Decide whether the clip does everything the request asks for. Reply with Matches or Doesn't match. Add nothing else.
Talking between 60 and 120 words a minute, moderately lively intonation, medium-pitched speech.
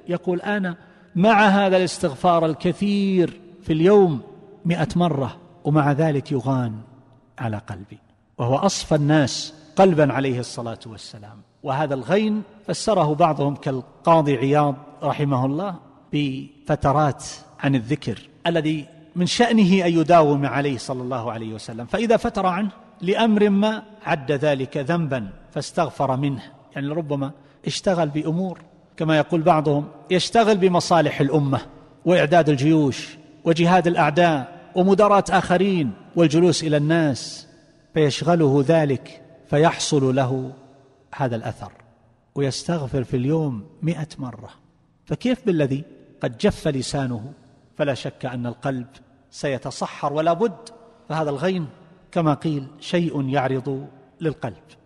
Matches